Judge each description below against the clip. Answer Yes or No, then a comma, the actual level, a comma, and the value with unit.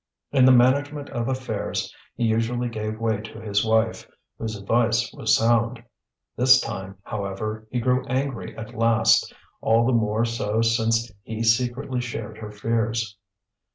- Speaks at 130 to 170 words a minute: Yes, average, 150 wpm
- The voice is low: Yes, low, 115 Hz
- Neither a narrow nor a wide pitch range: No, narrow, 1.9 semitones